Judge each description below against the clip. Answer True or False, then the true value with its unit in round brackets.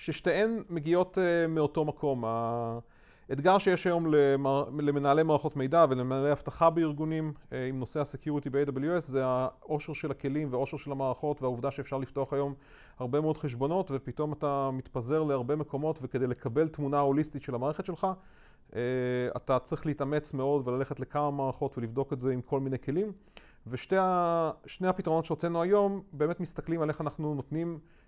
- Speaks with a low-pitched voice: False (145 Hz)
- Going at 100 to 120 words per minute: False (145 wpm)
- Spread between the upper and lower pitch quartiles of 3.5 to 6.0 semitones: False (2.9 semitones)